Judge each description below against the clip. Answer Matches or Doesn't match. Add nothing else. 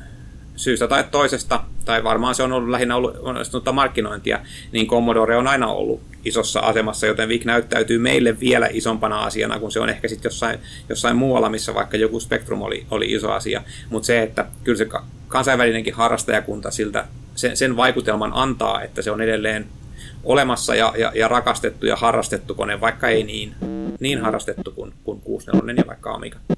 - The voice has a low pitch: Matches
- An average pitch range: Doesn't match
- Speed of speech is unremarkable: Doesn't match